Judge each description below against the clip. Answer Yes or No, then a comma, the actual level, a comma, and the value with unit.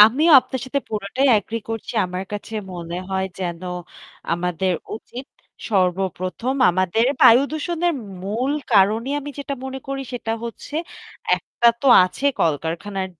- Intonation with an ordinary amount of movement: No, wide, 6.2 semitones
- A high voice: Yes, high, 215 Hz